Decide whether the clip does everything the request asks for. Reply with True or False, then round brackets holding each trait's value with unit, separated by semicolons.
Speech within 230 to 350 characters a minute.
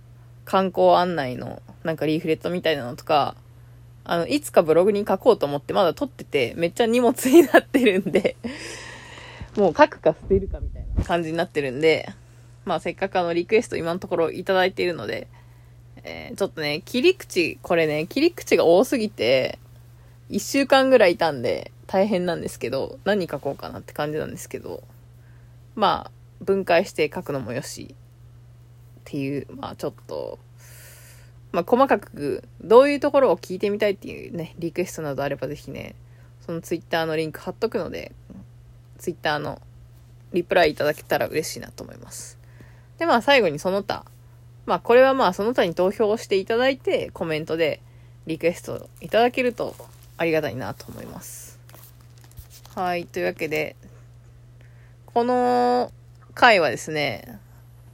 True (345 characters per minute)